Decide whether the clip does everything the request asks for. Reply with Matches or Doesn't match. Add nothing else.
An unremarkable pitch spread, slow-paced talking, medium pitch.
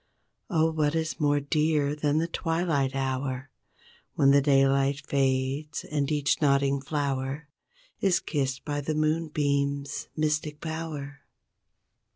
Doesn't match